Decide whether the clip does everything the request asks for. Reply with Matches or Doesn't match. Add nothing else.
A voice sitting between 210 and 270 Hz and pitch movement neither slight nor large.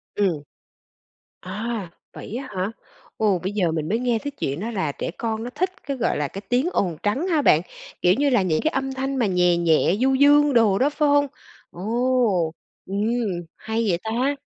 Doesn't match